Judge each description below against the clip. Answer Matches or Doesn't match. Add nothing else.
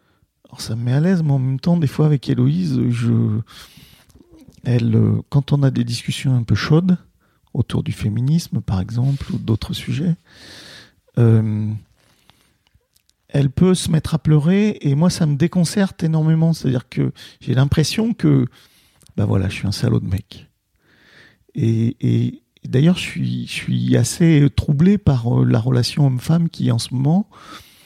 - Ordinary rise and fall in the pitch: Doesn't match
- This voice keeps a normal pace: Matches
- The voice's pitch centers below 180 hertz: Matches